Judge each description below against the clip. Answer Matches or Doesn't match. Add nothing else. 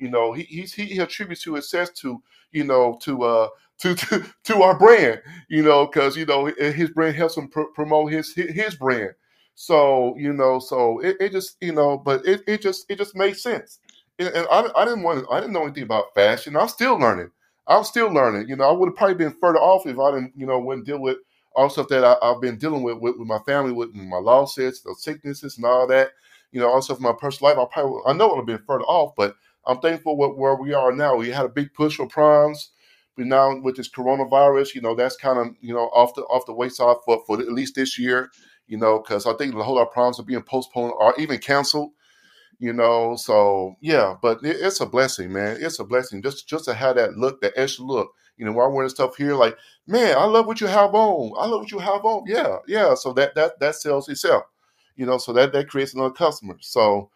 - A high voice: Doesn't match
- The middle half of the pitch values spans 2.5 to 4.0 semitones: Doesn't match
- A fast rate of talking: Matches